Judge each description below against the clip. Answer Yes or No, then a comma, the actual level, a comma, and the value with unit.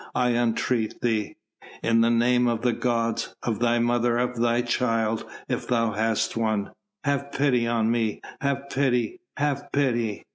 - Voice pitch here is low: Yes, low, 120 Hz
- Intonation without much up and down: Yes, narrow, 1.5 semitones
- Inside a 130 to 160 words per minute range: Yes, average, 155 wpm